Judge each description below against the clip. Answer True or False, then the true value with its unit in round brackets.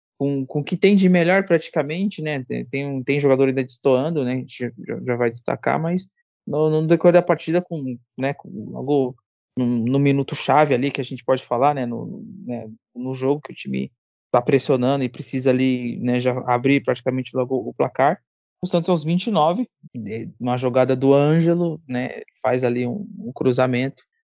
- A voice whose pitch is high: False (135 Hz)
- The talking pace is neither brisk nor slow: True (175 wpm)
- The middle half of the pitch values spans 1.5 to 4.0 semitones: False (4.4 semitones)